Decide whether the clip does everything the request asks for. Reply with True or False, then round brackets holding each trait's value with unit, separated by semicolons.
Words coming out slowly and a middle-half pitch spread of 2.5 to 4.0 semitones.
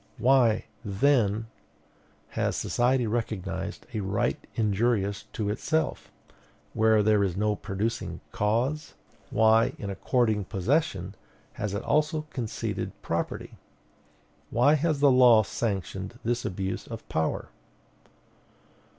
True (105 wpm; 3.6 semitones)